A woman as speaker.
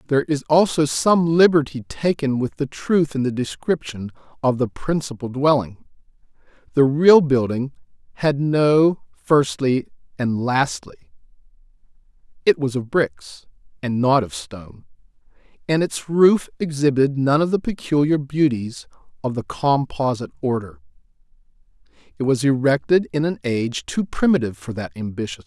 No: male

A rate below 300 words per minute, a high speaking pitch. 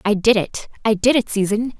Yes: average, 200 wpm; high, 215 Hz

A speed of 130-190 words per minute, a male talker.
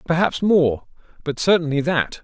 Yes: slow, 135 wpm; male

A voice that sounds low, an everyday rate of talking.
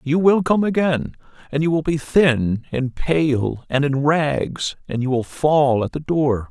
No: medium, 145 Hz; average, 195 wpm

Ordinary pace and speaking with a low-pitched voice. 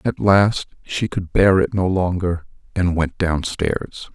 Yes: average, 160 wpm; very low, 90 Hz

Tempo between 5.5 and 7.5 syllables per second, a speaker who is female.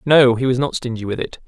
No: 6.0 syllables/s; male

